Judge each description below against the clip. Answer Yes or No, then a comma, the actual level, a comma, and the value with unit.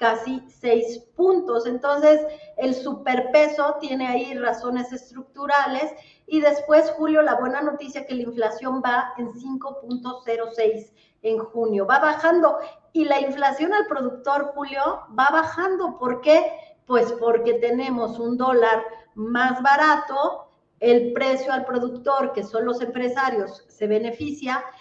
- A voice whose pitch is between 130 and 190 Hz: No, very high, 260 Hz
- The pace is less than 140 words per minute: Yes, average, 130 wpm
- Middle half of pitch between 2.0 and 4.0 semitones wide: Yes, average, 3.6 semitones